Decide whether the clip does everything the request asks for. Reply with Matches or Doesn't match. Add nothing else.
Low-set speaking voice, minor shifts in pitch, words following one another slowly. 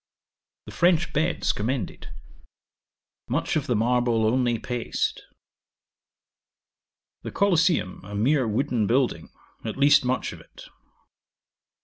Doesn't match